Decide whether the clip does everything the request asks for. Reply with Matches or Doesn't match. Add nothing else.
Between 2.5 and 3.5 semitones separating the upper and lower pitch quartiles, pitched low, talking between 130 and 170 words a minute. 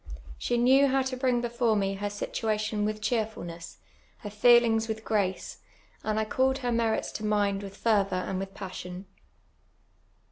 Doesn't match